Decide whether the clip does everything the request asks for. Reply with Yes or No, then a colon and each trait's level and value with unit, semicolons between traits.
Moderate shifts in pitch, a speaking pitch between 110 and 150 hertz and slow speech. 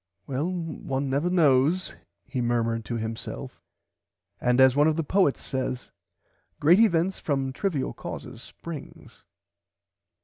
Yes: average, 4.6 semitones; medium, 140 Hz; slow, 125 wpm